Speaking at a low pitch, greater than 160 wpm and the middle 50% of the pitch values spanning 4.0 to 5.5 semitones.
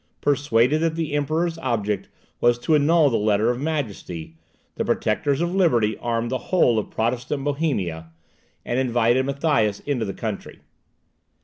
No: low, 125 Hz; average, 145 wpm; average, 4.9 semitones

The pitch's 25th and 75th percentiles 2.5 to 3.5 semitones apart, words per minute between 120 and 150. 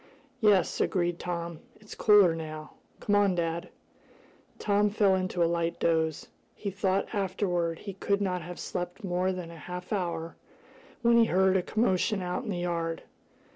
No: average, 2.9 semitones; average, 165 wpm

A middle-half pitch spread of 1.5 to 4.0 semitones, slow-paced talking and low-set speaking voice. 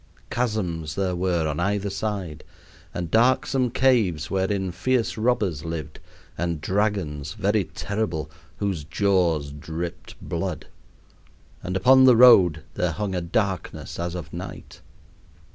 No: average, 4.4 semitones; slow, 125 wpm; very low, 95 Hz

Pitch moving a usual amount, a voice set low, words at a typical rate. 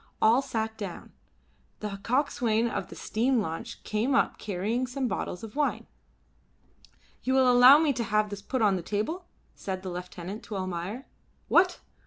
No: average, 4.5 semitones; high, 220 Hz; average, 165 wpm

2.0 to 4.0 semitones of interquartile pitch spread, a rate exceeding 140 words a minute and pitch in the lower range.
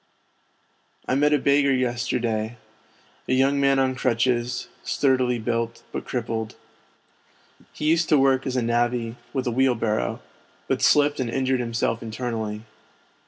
No: narrow, 2.4 semitones; slow, 135 wpm; low, 125 Hz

